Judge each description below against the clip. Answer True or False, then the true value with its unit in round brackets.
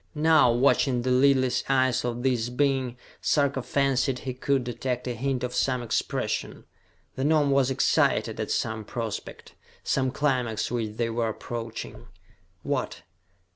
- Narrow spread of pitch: True (2.2 semitones)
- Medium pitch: False (125 Hz)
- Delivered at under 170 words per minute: True (140 wpm)